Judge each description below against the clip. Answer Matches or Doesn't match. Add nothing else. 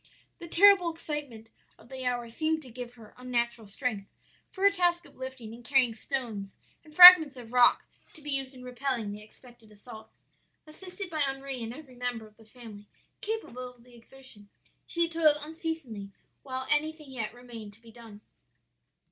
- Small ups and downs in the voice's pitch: Doesn't match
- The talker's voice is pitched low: Doesn't match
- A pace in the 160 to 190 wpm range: Matches